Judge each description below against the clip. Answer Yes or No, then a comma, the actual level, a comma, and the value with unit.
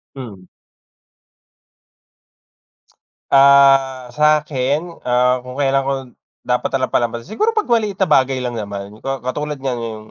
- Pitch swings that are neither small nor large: Yes, average, 3.1 semitones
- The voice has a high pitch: No, low, 135 Hz